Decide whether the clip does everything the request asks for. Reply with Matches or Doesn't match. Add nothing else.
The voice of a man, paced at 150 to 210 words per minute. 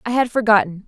Doesn't match